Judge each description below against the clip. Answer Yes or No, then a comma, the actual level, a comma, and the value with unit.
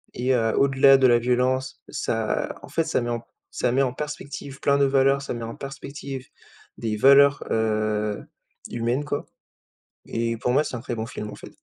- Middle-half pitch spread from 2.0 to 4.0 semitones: Yes, average, 3.0 semitones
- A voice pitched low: Yes, low, 125 Hz